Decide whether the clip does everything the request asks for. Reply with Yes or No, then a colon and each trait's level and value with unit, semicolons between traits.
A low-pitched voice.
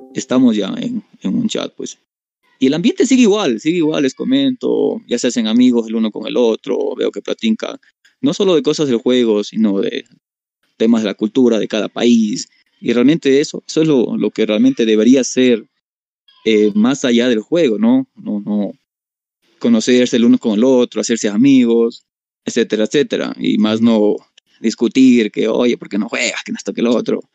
Yes: low, 125 Hz